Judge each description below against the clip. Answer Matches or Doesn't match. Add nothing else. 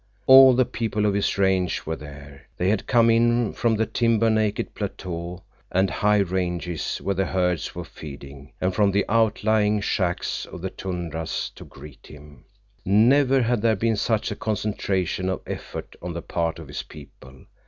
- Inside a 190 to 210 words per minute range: Doesn't match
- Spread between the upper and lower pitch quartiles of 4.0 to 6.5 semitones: Matches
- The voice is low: Matches